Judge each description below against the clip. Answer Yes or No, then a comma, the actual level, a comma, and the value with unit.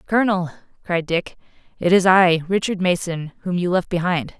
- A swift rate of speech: No, average, 165 wpm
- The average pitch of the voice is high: No, medium, 180 Hz